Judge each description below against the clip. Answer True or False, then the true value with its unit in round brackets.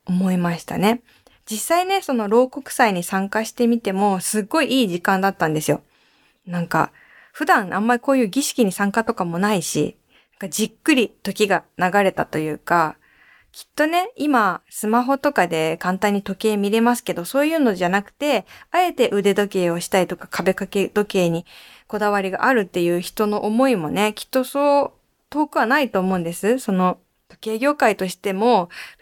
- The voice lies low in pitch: False (210 Hz)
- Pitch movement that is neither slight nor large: True (5.0 semitones)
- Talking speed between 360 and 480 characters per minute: False (350 characters per minute)